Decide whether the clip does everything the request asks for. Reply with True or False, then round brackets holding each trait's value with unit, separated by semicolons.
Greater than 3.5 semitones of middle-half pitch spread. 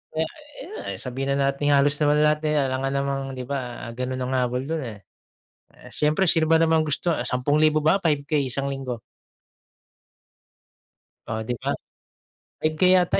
False (3.1 semitones)